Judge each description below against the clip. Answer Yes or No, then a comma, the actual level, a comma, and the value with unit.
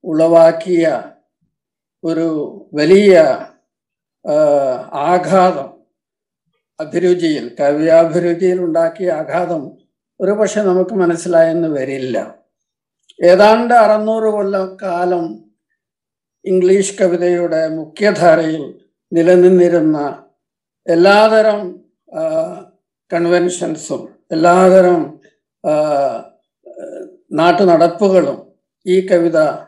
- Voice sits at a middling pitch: Yes, medium, 180 Hz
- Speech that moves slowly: Yes, slow, 55 wpm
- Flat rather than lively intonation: No, average, 3.2 semitones